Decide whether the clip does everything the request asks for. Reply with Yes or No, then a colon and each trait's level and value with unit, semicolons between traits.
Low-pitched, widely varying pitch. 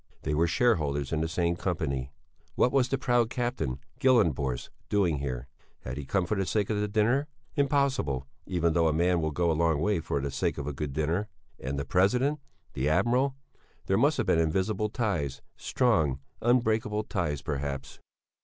Yes: very low, 85 Hz; wide, 7.2 semitones